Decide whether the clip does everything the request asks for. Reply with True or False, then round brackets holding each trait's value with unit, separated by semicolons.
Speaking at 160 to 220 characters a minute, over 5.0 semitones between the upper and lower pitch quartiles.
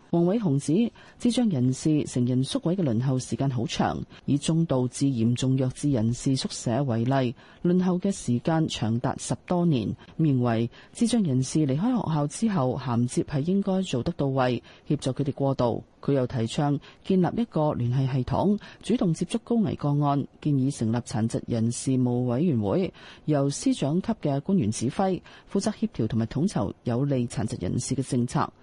False (270 characters per minute; 5.5 semitones)